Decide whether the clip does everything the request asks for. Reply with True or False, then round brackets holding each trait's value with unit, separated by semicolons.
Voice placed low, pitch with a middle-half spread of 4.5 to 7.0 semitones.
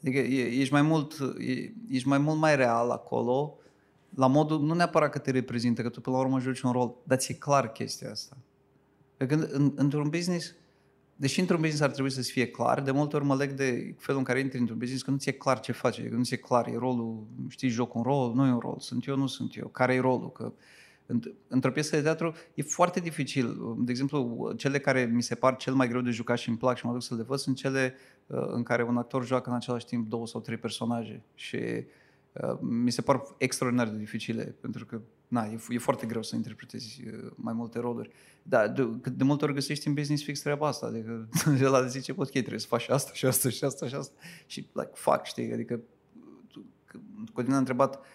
False (130 Hz; 2.8 semitones)